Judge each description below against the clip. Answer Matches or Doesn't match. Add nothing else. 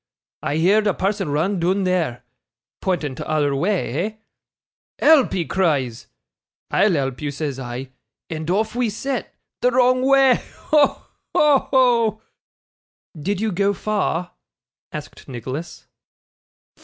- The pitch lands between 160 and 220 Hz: Matches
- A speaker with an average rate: Doesn't match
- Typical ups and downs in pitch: Doesn't match